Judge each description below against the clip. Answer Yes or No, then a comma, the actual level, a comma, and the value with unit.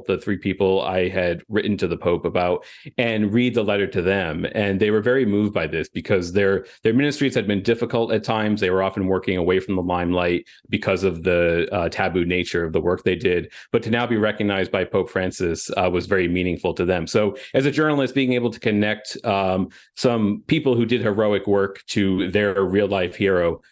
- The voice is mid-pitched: No, low, 100 Hz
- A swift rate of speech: Yes, fast, 215 wpm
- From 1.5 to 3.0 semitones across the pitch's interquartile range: No, average, 3.5 semitones